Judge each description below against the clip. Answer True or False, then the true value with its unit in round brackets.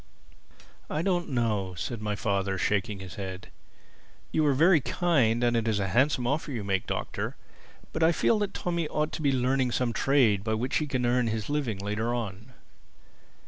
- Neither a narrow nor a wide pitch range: False (5.7 semitones)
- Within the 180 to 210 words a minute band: True (185 wpm)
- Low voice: True (120 Hz)